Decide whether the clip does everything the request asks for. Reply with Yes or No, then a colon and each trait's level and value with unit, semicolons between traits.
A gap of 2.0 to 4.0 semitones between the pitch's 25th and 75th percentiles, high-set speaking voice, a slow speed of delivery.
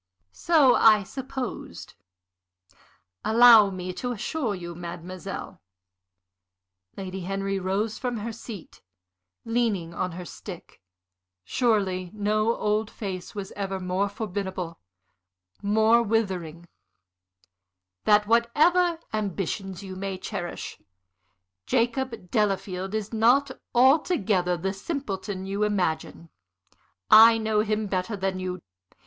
Yes: average, 3.4 semitones; high, 205 Hz; slow, 105 wpm